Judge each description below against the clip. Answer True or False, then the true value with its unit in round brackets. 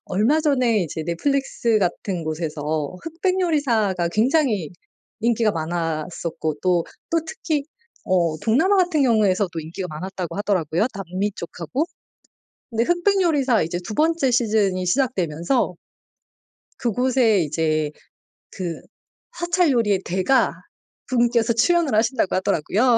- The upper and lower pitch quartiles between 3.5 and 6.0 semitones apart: False (7.5 semitones)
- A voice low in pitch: False (215 Hz)